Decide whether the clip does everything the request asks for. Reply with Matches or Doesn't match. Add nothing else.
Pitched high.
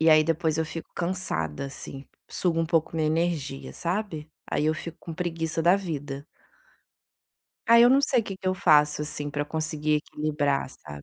Doesn't match